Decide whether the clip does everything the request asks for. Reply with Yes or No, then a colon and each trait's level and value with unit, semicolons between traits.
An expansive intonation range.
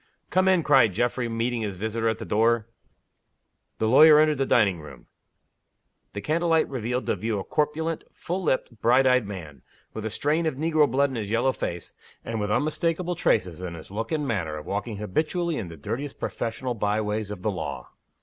Yes: wide, 6.3 semitones